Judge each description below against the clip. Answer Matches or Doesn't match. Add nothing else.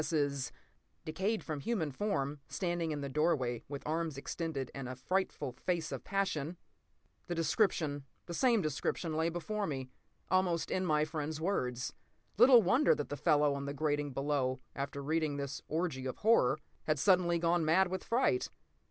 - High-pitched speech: Doesn't match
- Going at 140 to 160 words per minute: Matches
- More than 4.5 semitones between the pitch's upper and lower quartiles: Doesn't match